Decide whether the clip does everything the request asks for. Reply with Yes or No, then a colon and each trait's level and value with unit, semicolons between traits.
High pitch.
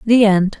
Yes: high, 210 Hz